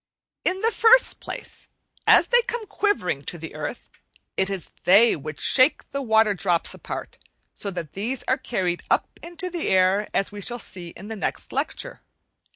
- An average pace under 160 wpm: No, average, 175 wpm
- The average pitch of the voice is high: Yes, high, 210 Hz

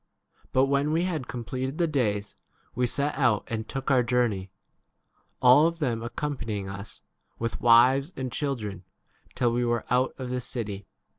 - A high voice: No, low, 125 Hz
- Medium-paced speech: Yes, average, 170 wpm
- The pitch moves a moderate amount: Yes, average, 3.2 semitones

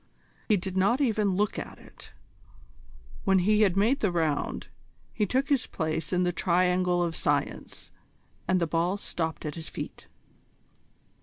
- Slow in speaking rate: No, average, 155 wpm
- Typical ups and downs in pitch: Yes, average, 3.5 semitones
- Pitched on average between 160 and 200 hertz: Yes, medium, 185 Hz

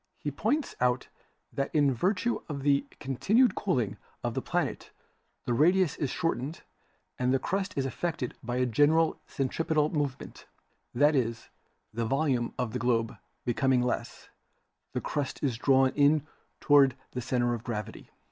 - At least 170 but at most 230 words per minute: No, average, 150 wpm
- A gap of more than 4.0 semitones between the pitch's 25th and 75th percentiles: No, average, 3.7 semitones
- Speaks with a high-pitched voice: No, low, 135 Hz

